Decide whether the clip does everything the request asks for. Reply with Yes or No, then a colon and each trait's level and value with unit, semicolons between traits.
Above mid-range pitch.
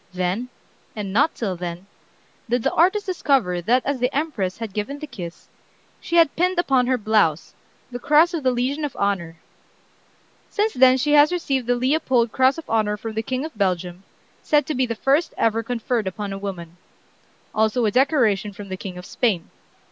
Yes: high, 240 Hz